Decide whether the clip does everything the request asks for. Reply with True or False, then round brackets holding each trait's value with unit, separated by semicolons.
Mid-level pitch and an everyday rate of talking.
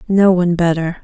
True (175 Hz; 175 wpm)